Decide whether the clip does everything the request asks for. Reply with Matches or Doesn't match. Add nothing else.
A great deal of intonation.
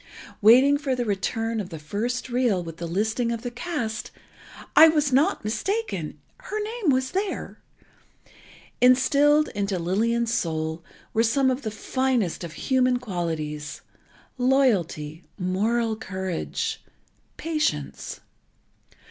Matches